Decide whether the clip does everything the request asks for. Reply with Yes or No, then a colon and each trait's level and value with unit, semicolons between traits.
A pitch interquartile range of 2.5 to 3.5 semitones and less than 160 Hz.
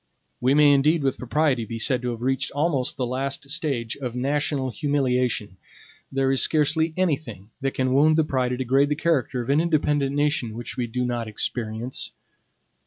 Yes: average, 3.0 semitones; low, 135 Hz